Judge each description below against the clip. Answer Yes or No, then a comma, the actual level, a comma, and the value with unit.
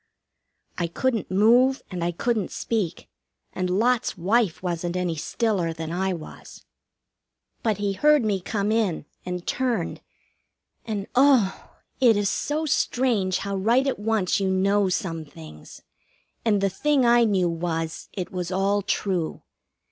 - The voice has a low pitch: No, high, 200 Hz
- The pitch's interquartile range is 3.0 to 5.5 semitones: Yes, average, 4.3 semitones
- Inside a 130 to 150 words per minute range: Yes, average, 145 wpm